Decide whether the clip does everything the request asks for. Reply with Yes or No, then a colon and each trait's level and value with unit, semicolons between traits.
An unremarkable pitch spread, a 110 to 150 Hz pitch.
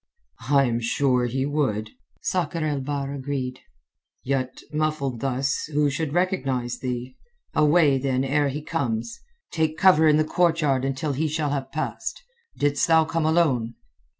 Yes: average, 3.0 semitones; medium, 140 Hz